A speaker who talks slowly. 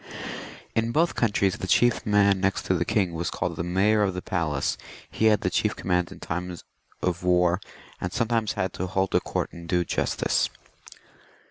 No: average, 190 wpm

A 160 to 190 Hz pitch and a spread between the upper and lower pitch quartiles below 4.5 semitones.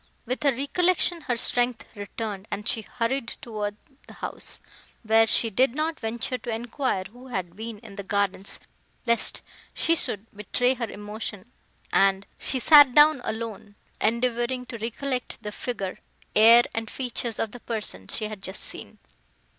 No: high, 230 Hz; average, 3.1 semitones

